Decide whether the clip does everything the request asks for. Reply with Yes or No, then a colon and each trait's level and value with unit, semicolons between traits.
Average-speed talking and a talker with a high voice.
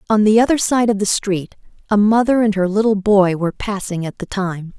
No: fast, 225 wpm; high, 205 Hz